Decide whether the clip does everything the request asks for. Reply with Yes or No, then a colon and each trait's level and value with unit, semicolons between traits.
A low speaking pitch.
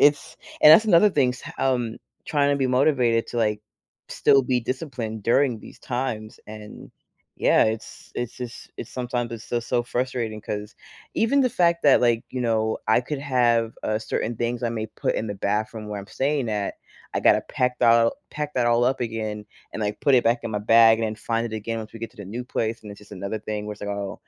Yes: low, 115 Hz